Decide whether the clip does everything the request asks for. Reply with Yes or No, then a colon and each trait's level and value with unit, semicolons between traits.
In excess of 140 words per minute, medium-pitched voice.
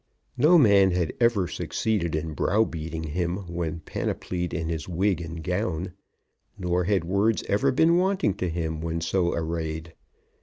No: average, 150 wpm; very low, 90 Hz